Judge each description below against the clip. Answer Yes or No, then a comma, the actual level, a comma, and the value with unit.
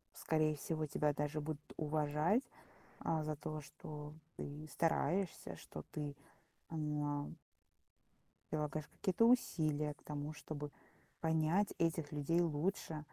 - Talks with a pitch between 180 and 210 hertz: No, medium, 155 Hz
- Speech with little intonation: Yes, narrow, 1.5 semitones